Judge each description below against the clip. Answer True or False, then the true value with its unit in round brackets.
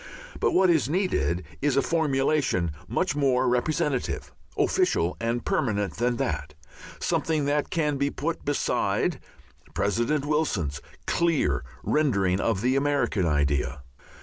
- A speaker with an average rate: False (120 wpm)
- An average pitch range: False (7.6 semitones)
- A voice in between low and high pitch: False (130 Hz)